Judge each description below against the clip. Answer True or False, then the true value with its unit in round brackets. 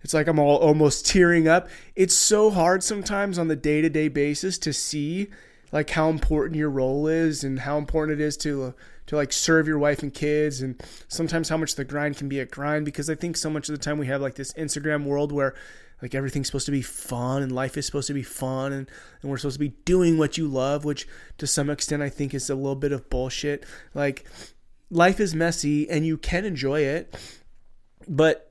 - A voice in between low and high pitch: True (150 Hz)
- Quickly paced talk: True (225 wpm)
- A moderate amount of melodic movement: False (2.2 semitones)